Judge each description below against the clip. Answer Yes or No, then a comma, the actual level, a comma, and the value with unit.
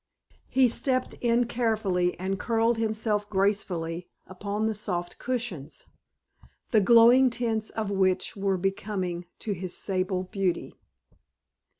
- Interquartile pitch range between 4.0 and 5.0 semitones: No, average, 3.6 semitones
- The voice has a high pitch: Yes, high, 205 Hz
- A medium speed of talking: No, slow, 120 wpm